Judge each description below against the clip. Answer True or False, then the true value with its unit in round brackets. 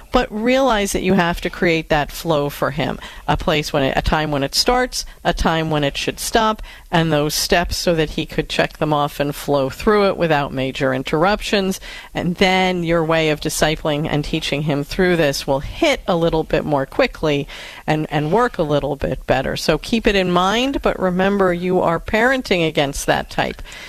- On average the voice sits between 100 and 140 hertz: False (165 Hz)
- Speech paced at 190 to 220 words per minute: True (205 wpm)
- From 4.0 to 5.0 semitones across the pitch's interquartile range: True (4.6 semitones)